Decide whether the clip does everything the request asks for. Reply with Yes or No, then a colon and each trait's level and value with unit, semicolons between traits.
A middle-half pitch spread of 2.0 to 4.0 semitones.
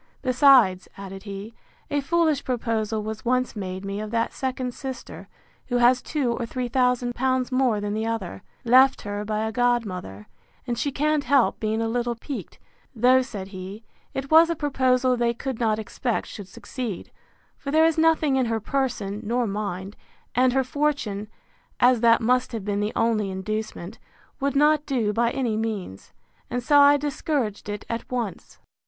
Yes: average, 3.7 semitones